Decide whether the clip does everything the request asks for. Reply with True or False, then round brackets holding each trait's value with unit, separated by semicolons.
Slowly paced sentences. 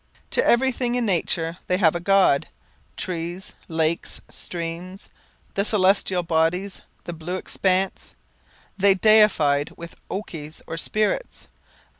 True (115 wpm)